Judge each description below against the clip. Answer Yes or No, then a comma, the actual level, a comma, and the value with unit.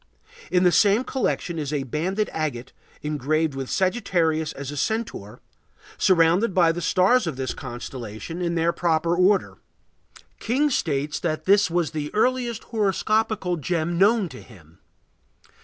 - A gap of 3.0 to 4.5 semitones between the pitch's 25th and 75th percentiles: No, average, 5.0 semitones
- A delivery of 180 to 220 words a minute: No, average, 140 wpm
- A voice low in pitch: No, medium, 170 Hz